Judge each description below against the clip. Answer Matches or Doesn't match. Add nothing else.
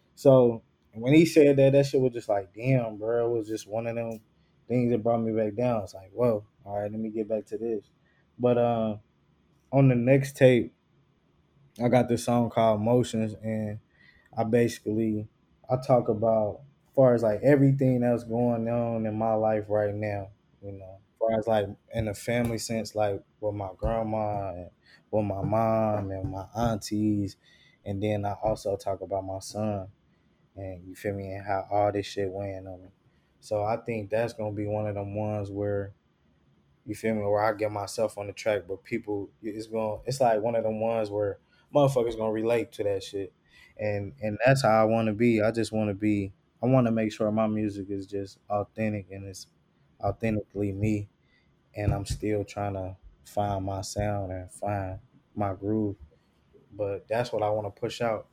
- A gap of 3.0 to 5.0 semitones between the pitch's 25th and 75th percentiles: Doesn't match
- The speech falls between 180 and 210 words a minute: Matches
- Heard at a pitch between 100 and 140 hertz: Matches